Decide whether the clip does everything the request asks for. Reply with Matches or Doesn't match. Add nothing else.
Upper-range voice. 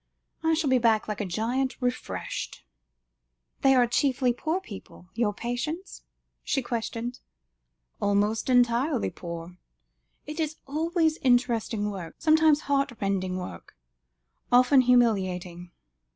Matches